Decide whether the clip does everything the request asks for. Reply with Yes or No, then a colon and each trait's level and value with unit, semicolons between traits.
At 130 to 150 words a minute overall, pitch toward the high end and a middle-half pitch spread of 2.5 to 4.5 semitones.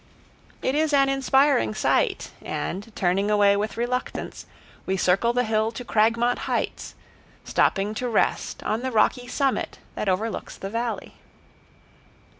Yes: slow, 135 wpm; high, 225 Hz; average, 3.6 semitones